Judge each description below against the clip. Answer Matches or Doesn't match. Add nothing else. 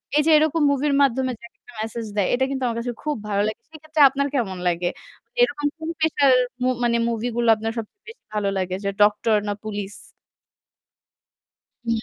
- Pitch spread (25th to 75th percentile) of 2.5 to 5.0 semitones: Doesn't match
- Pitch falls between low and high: Doesn't match